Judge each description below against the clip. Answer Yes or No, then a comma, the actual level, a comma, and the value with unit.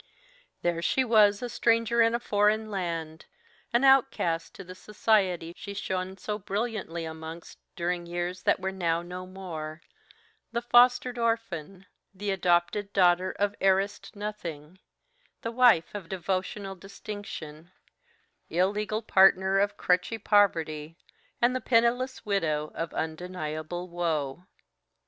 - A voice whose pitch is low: No, high, 190 Hz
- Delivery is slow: Yes, slow, 125 wpm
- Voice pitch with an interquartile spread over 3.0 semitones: Yes, average, 3.7 semitones